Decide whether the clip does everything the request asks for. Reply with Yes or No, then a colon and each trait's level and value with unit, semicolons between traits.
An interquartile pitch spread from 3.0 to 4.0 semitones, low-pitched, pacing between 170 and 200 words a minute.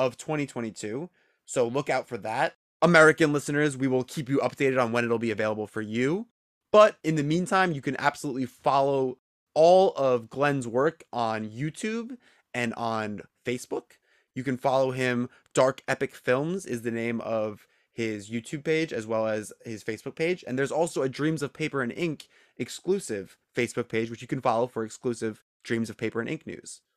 No: average, 4.7 semitones; low, 130 Hz; average, 180 wpm